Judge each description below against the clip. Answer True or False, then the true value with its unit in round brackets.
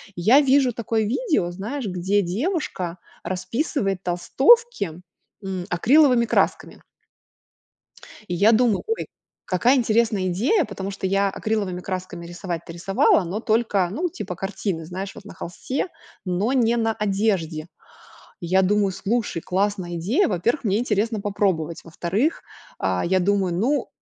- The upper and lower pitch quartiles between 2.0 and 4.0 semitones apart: False (4.5 semitones)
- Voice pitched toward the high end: True (200 Hz)